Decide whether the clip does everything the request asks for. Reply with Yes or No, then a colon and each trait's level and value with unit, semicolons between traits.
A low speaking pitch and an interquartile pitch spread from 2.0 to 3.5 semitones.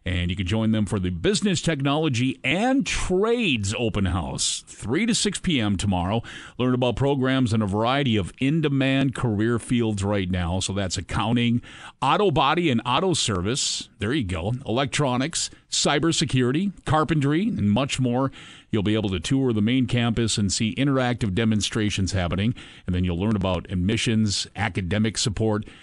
No: low, 115 Hz; average, 4.9 semitones